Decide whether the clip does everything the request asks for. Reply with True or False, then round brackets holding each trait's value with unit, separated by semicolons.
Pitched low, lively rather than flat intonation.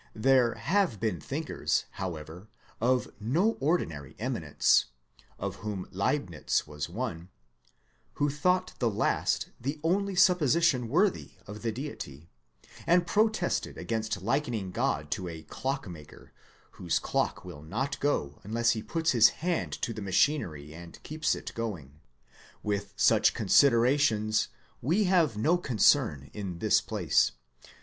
True (115 Hz; 8.3 semitones)